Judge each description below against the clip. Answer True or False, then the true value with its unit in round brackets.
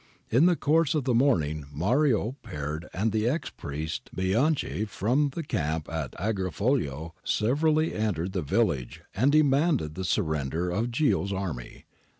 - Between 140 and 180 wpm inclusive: True (145 wpm)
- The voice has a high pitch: False (105 Hz)